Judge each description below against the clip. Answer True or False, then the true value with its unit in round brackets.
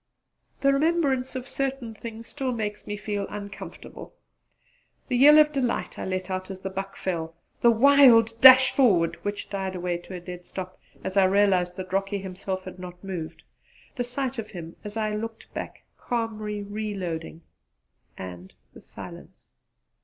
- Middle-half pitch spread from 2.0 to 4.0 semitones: False (4.4 semitones)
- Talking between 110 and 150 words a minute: False (160 wpm)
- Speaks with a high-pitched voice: True (205 Hz)